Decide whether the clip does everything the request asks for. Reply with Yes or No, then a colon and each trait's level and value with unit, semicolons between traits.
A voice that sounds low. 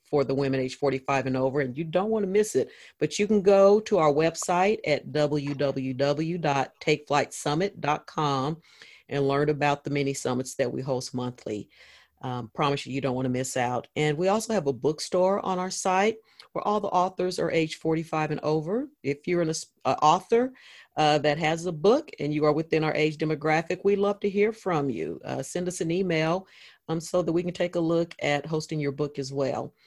No: medium, 155 Hz